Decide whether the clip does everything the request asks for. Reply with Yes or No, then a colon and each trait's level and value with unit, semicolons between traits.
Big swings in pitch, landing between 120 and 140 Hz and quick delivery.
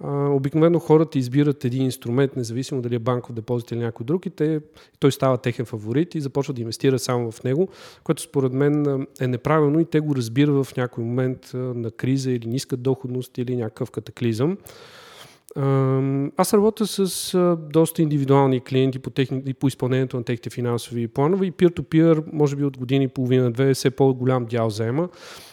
No: average, 3.3 semitones; low, 135 Hz; fast, 170 wpm